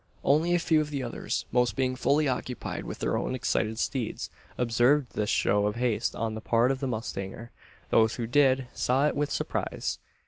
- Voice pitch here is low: Yes, low, 125 Hz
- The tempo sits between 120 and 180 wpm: No, average, 195 wpm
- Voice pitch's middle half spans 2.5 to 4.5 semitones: Yes, average, 3.5 semitones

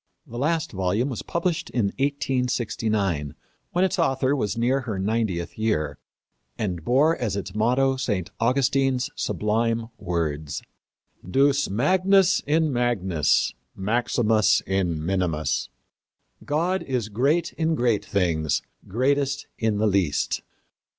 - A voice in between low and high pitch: No, low, 115 Hz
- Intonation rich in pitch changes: Yes, wide, 6.1 semitones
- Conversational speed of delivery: No, slow, 115 wpm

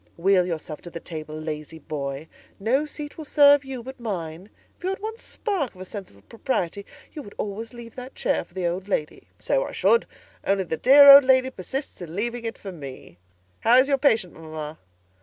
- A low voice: No, high, 200 Hz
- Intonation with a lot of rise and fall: Yes, wide, 8.4 semitones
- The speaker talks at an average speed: No, fast, 210 wpm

